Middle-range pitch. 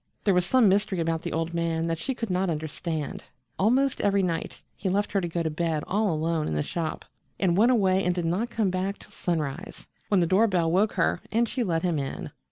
Yes: medium, 180 Hz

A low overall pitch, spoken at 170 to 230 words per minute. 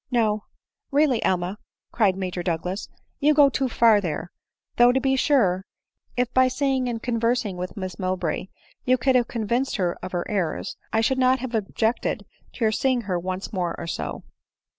No: high, 225 Hz; average, 195 wpm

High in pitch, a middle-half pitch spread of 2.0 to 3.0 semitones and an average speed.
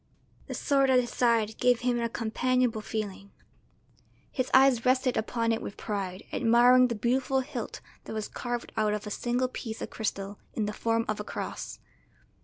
Yes: high, 235 Hz; average, 2.7 semitones; average, 180 wpm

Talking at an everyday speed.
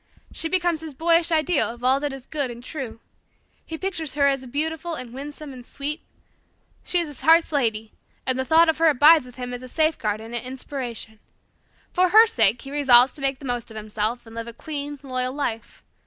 No: fast, 215 wpm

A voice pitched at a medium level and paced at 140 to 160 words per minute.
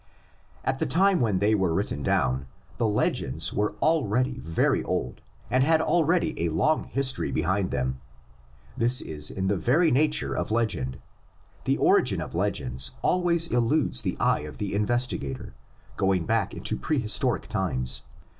No: low, 105 Hz; average, 150 wpm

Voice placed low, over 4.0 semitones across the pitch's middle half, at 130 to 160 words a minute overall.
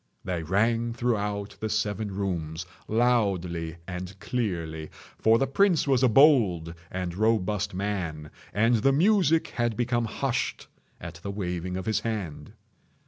Yes: low, 105 Hz; average, 4.7 semitones; slow, 135 wpm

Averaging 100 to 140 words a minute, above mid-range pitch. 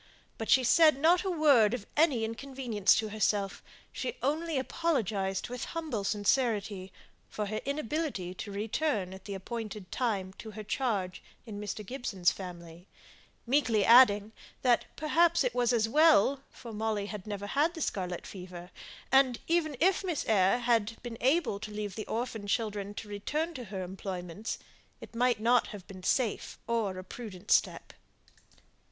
No: average, 160 wpm; high, 220 Hz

